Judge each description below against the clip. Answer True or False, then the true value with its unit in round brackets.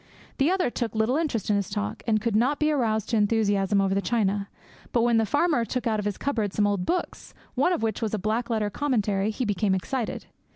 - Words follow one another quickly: True (235 wpm)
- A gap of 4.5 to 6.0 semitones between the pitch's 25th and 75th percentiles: False (3.4 semitones)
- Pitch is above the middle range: True (220 Hz)